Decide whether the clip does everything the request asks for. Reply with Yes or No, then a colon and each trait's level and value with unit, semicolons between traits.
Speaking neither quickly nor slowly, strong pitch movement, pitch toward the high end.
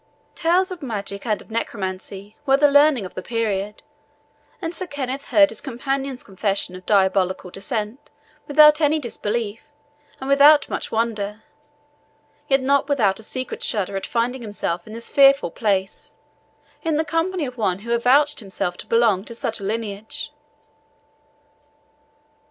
Yes: average, 150 wpm; wide, 5.7 semitones; high, 230 Hz